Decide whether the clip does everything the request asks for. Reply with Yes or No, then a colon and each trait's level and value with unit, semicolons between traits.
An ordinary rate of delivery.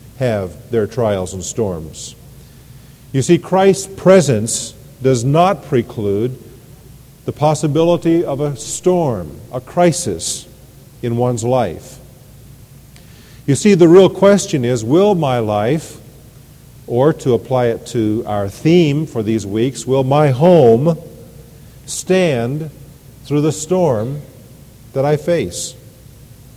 No: slow, 115 wpm